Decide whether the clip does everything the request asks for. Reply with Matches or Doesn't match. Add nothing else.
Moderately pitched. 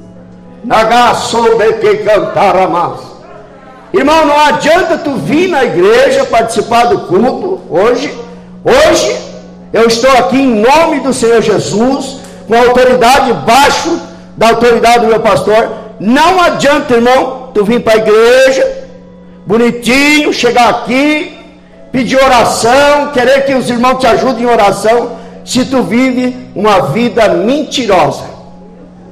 Doesn't match